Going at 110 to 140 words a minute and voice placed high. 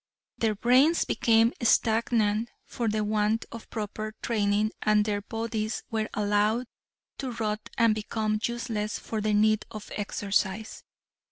Yes: slow, 135 wpm; high, 215 Hz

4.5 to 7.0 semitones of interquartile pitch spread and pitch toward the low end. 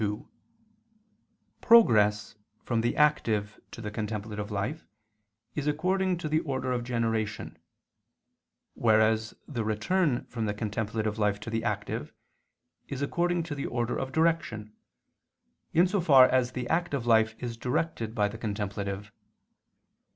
Yes: wide, 5.4 semitones; low, 115 Hz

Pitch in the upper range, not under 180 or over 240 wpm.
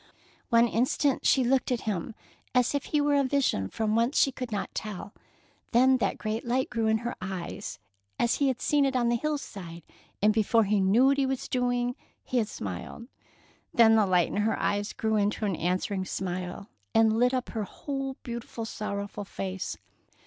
Yes: high, 225 Hz; average, 190 wpm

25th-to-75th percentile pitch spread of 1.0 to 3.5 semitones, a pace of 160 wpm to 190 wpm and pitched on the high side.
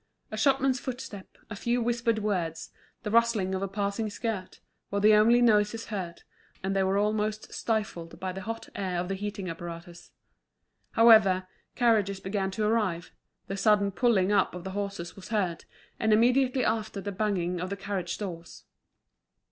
Yes: average, 2.7 semitones; average, 165 wpm; high, 205 Hz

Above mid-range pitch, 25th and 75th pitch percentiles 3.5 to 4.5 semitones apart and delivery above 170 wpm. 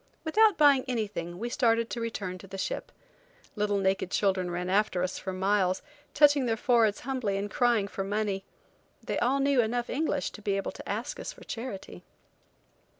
Yes: high, 210 Hz; average, 4.1 semitones; average, 180 wpm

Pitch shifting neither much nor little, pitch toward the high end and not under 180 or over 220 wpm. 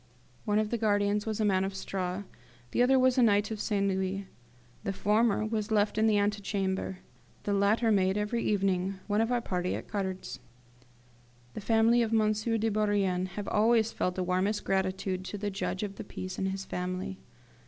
No: narrow, 2.2 semitones; high, 205 Hz; average, 190 wpm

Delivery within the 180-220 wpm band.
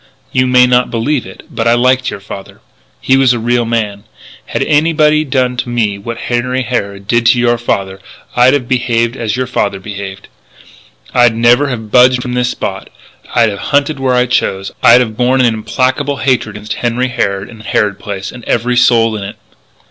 Yes: average, 195 wpm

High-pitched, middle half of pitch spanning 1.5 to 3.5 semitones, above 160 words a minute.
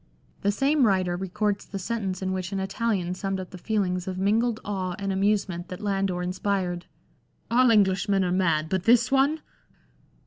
Yes: high, 195 Hz; narrow, 2.4 semitones; average, 180 wpm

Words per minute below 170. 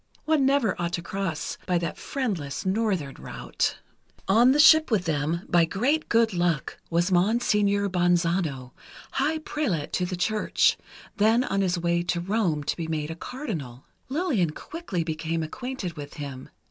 Yes: average, 160 wpm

